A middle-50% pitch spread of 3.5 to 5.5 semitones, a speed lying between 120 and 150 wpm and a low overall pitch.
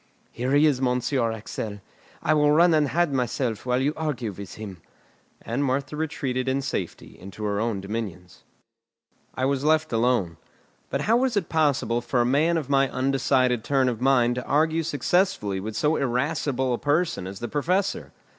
No: average, 4.5 semitones; average, 175 wpm; low, 130 Hz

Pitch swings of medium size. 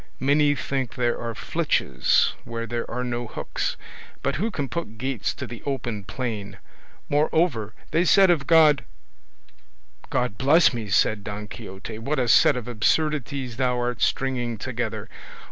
Yes: average, 4.0 semitones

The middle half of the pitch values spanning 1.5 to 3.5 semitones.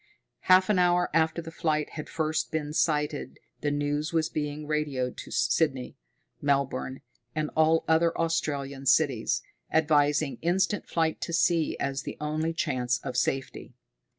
Yes: narrow, 2.6 semitones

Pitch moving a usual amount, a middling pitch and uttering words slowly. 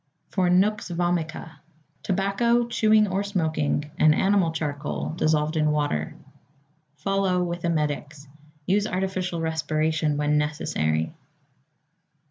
Yes: average, 4.0 semitones; medium, 165 Hz; slow, 100 wpm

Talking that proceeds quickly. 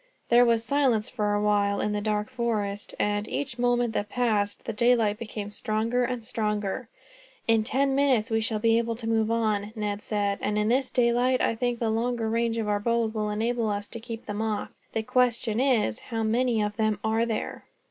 Yes: fast, 210 wpm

